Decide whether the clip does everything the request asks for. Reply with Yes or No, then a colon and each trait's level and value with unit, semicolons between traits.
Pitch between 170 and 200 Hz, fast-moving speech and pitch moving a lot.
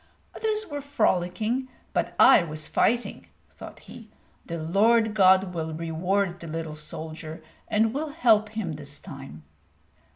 No: medium, 185 Hz; slow, 135 wpm; wide, 5.8 semitones